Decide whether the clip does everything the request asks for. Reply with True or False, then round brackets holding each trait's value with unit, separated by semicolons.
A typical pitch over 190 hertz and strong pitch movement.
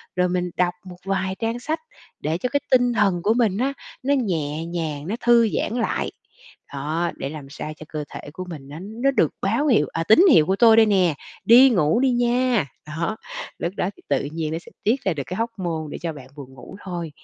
False (185 Hz; 6.6 semitones)